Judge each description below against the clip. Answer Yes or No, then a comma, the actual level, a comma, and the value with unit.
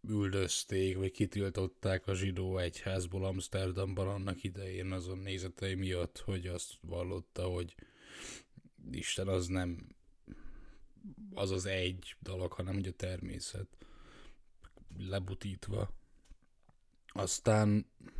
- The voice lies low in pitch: Yes, very low, 95 Hz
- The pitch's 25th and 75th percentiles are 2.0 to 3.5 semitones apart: No, narrow, 1.3 semitones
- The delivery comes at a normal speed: No, slow, 95 wpm